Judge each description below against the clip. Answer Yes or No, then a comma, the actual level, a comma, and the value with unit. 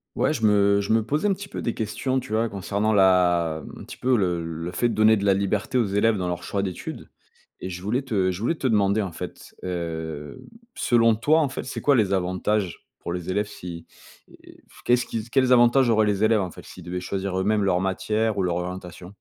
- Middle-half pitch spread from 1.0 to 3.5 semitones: No, average, 3.9 semitones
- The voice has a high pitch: No, low, 100 Hz